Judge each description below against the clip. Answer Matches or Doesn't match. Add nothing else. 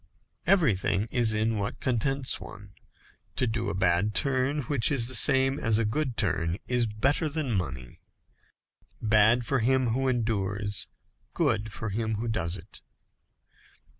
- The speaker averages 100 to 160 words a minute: Matches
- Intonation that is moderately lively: Matches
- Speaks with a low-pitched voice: Matches